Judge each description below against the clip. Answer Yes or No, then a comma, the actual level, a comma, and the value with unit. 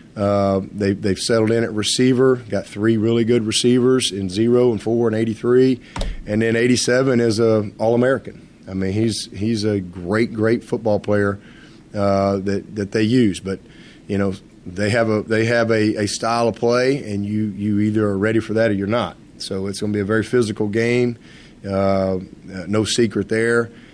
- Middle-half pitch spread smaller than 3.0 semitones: Yes, narrow, 2.6 semitones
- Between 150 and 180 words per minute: No, average, 190 wpm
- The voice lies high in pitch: No, low, 110 Hz